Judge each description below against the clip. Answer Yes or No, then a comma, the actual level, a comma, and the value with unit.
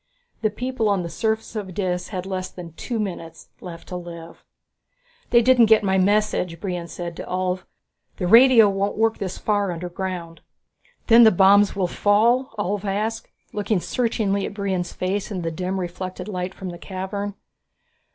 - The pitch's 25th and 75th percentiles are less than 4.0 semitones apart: Yes, average, 2.9 semitones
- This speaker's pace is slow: No, average, 170 wpm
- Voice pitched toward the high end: Yes, high, 195 Hz